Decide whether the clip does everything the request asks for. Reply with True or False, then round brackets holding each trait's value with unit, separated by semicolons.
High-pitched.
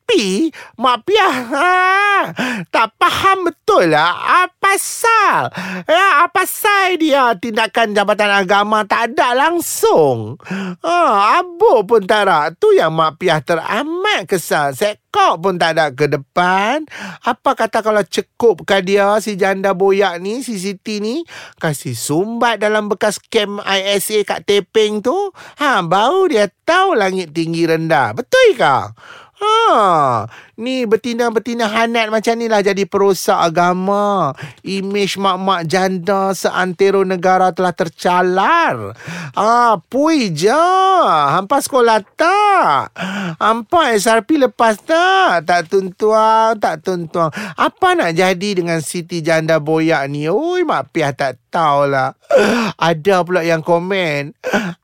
True (210 Hz)